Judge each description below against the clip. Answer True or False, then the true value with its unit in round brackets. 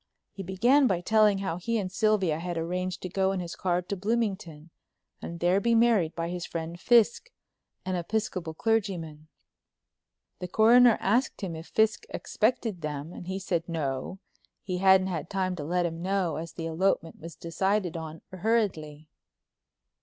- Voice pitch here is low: False (185 Hz)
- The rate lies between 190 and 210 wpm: False (165 wpm)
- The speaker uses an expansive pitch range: False (3.8 semitones)